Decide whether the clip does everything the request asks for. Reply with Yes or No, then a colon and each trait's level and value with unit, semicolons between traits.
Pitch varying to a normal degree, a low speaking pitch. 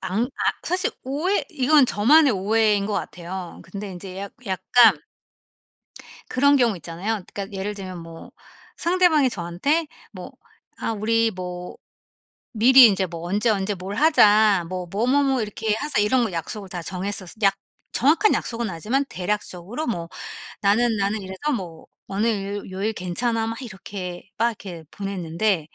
No: average, 4.4 semitones; high, 205 Hz